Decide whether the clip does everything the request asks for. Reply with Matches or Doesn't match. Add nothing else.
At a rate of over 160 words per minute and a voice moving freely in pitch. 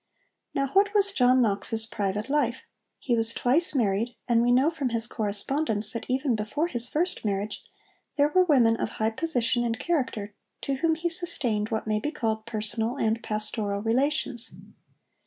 Doesn't match